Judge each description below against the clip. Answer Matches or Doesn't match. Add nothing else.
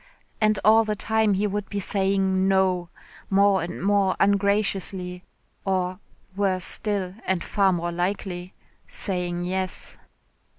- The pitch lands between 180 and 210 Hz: Matches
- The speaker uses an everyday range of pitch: Doesn't match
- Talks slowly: Matches